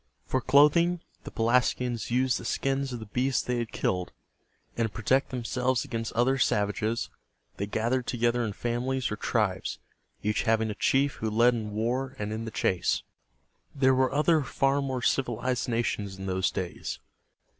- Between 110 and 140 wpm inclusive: No, average, 165 wpm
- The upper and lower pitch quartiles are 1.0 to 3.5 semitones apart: Yes, average, 3.0 semitones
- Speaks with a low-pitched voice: Yes, low, 120 Hz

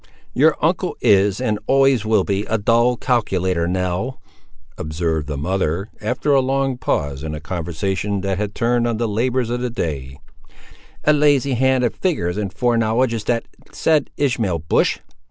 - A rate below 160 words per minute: No, average, 165 wpm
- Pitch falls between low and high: No, low, 110 Hz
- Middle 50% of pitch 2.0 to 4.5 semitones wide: No, wide, 5.5 semitones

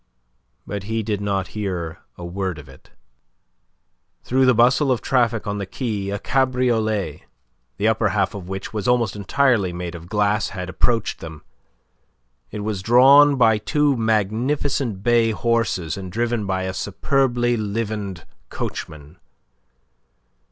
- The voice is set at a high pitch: No, low, 105 Hz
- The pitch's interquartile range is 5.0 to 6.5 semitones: No, average, 3.9 semitones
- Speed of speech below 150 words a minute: Yes, average, 140 wpm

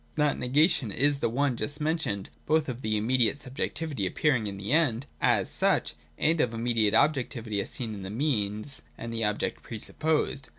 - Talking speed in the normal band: Yes, average, 185 wpm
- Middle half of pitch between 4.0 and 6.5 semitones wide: Yes, average, 5.1 semitones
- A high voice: No, low, 125 Hz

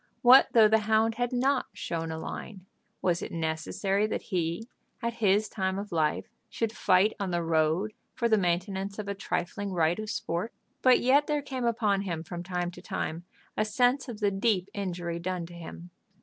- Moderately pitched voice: No, high, 195 Hz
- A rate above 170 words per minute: Yes, average, 190 wpm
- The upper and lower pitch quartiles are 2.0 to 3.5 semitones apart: No, average, 4.2 semitones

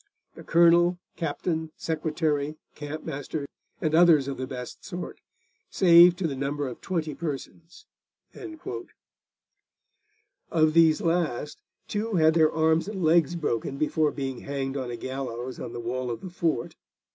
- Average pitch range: Yes, average, 3.6 semitones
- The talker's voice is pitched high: No, medium, 155 Hz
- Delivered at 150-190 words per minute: No, average, 140 wpm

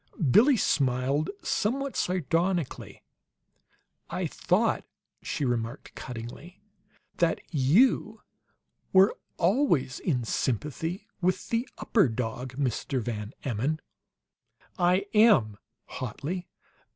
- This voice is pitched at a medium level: Yes, medium, 155 Hz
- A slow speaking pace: Yes, slow, 90 wpm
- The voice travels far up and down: Yes, wide, 7.3 semitones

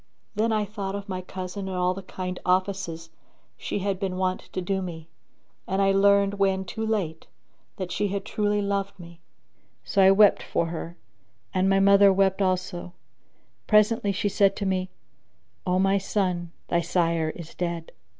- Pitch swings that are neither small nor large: No, narrow, 1.7 semitones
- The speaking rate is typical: Yes, average, 170 wpm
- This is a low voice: No, high, 190 Hz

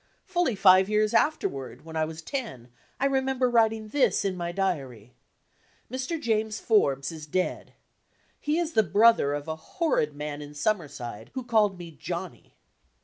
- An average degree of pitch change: No, wide, 7.7 semitones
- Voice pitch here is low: No, high, 190 Hz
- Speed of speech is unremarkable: Yes, average, 160 wpm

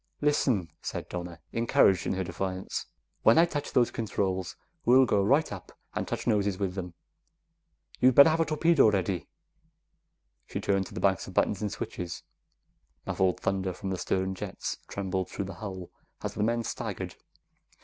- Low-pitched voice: Yes, low, 100 Hz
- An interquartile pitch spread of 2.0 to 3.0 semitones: No, average, 4.0 semitones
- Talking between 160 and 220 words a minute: Yes, average, 170 wpm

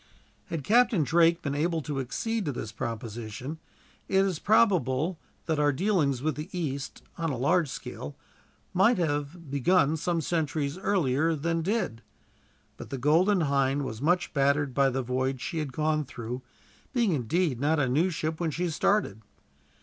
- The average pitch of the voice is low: No, medium, 155 Hz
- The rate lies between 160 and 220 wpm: Yes, average, 165 wpm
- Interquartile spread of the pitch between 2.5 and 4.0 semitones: No, average, 4.5 semitones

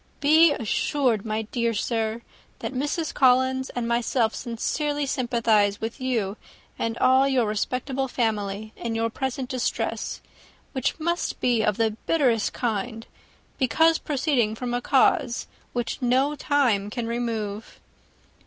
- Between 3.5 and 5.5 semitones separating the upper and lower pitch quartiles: No, average, 3.0 semitones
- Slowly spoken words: Yes, slow, 130 wpm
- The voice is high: Yes, high, 240 Hz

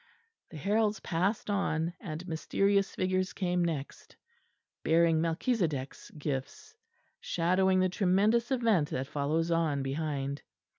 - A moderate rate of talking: No, slow, 110 wpm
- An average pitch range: Yes, average, 4.2 semitones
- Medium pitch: Yes, medium, 170 Hz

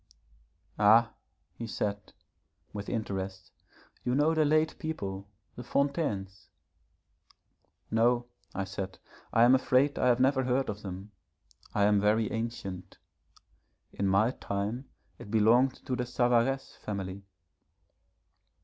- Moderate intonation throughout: Yes, average, 4.2 semitones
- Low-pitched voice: Yes, low, 115 Hz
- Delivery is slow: Yes, slow, 120 wpm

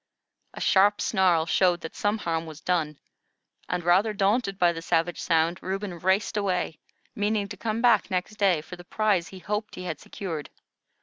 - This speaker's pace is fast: No, average, 180 wpm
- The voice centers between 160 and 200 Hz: Yes, medium, 185 Hz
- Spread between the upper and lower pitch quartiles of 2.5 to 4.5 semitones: Yes, average, 3.3 semitones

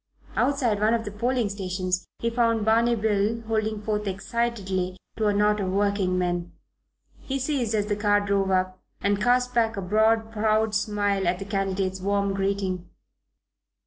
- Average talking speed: Yes, average, 165 wpm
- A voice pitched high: Yes, high, 205 Hz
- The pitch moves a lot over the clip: No, narrow, 2.4 semitones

